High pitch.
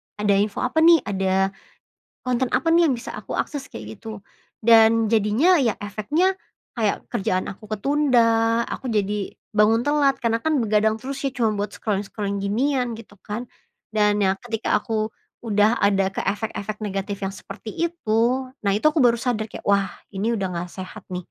Yes: high, 220 Hz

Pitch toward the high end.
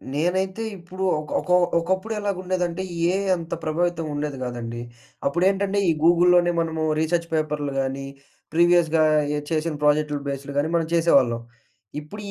No: medium, 165 Hz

